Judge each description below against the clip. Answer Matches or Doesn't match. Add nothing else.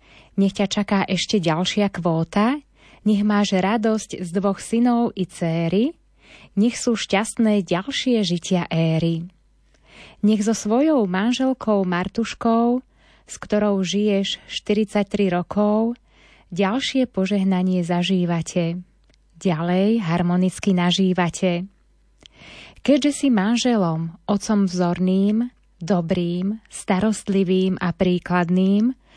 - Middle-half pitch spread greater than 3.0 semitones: Matches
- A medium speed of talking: Doesn't match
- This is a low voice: Doesn't match